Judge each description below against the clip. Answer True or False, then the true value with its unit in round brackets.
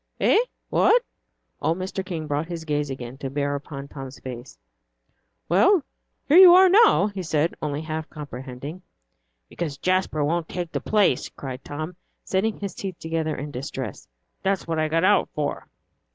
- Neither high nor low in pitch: True (160 Hz)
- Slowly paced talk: False (165 wpm)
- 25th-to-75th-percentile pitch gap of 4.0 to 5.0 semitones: True (4.7 semitones)